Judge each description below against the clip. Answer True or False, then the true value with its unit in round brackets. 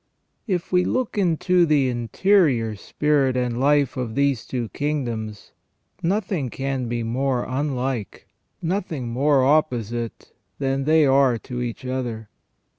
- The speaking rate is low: True (125 wpm)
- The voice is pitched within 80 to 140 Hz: True (135 Hz)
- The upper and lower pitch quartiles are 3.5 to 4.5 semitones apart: True (4.0 semitones)